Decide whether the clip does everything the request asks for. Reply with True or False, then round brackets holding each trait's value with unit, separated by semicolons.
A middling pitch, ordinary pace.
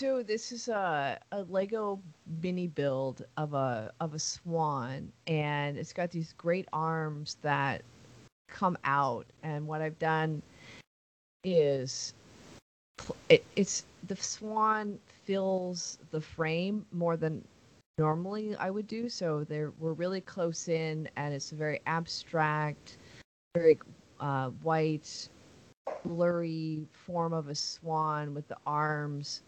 False (160 Hz; 125 wpm)